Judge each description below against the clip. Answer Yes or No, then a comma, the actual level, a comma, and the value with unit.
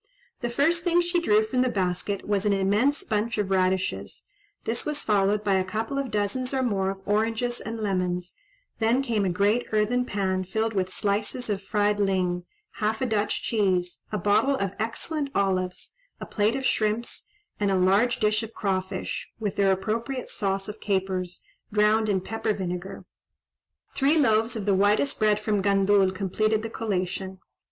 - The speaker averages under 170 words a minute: No, average, 175 wpm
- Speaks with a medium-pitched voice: No, high, 210 Hz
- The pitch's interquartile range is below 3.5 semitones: Yes, average, 2.8 semitones